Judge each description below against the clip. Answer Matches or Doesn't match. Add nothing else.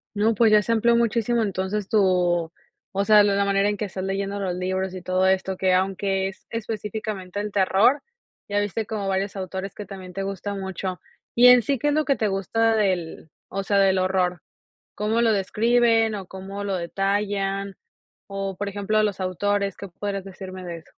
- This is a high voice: Matches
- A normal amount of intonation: Doesn't match